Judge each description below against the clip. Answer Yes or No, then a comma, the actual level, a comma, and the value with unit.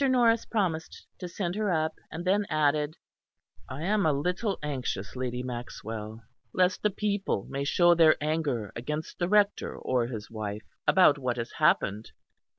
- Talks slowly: No, average, 155 wpm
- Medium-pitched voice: Yes, medium, 155 Hz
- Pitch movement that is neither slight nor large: No, wide, 7.1 semitones